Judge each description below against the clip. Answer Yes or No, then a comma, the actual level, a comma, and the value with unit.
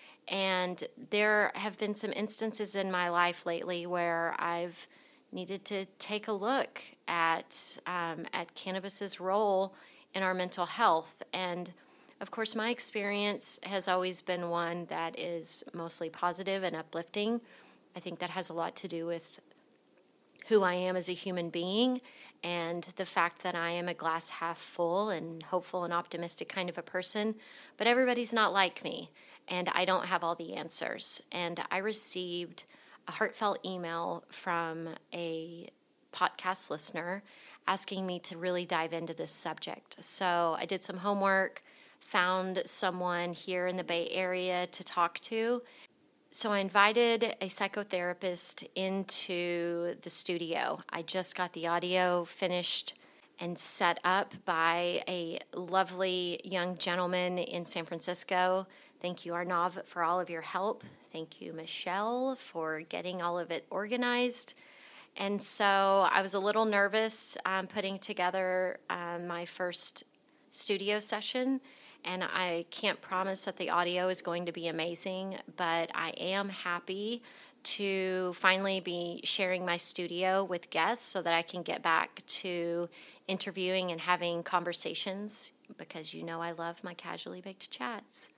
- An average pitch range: No, narrow, 2.3 semitones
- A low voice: No, medium, 180 Hz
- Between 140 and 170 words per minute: Yes, average, 150 wpm